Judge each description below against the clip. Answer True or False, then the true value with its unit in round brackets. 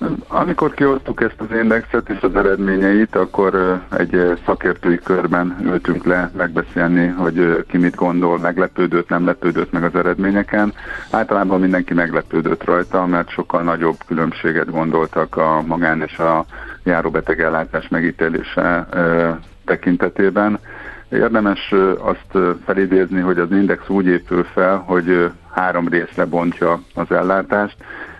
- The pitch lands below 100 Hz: True (90 Hz)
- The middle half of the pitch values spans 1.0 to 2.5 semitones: True (2.2 semitones)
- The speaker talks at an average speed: True (120 wpm)